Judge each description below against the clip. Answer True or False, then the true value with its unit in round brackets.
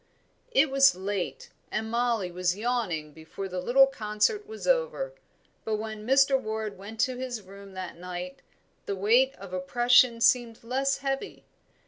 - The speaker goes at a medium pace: True (150 wpm)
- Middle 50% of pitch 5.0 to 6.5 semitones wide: True (5.4 semitones)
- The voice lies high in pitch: True (220 Hz)